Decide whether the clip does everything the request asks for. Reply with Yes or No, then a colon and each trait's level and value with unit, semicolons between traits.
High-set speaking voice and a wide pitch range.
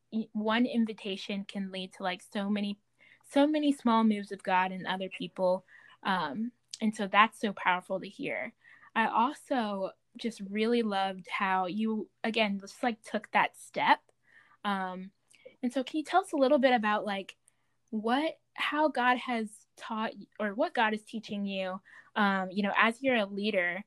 No: high, 215 Hz; average, 3.6 semitones